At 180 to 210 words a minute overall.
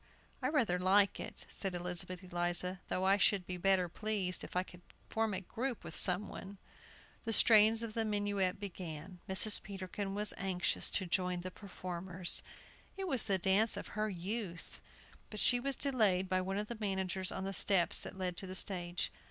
Yes: average, 185 wpm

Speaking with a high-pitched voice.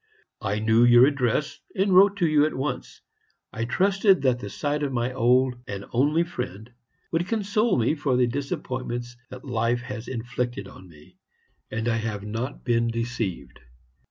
No: low, 125 Hz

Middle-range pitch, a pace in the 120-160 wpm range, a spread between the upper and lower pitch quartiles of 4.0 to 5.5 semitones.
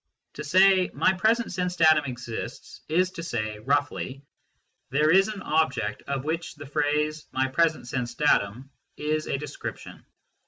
Yes: medium, 150 Hz; average, 155 wpm; average, 5.1 semitones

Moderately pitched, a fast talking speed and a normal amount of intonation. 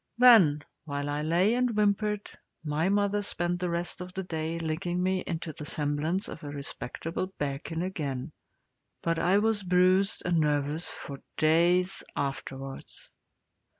No: medium, 170 Hz; average, 145 wpm; average, 4.0 semitones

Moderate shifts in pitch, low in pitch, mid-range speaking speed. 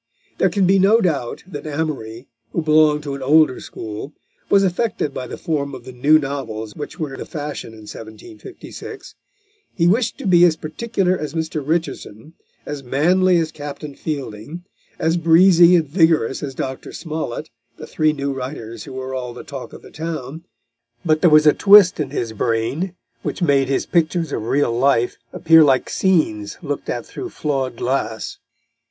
No: average, 4.3 semitones; medium, 150 Hz; average, 175 wpm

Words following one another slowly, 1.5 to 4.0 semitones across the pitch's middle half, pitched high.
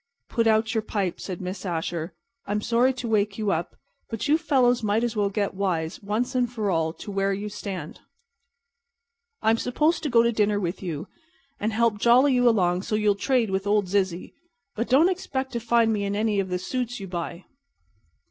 No: average, 195 wpm; average, 3.5 semitones; high, 210 Hz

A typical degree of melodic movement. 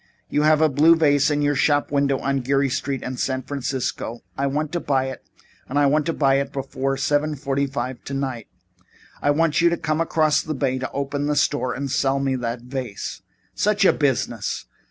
No: narrow, 1.9 semitones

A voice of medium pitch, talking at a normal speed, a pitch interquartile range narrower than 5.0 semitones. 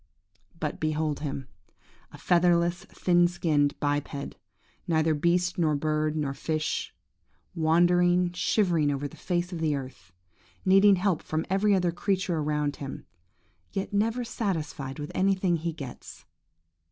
No: medium, 165 Hz; slow, 125 wpm; average, 3.4 semitones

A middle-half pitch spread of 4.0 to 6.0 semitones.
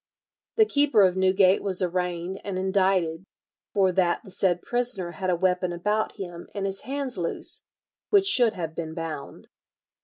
No: average, 2.8 semitones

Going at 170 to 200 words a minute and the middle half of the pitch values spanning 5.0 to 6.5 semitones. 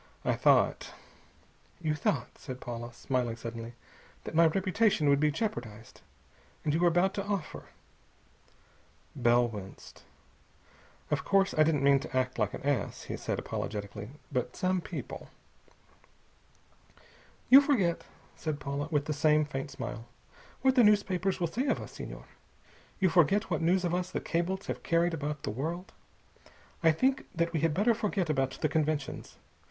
No: average, 160 wpm; wide, 5.4 semitones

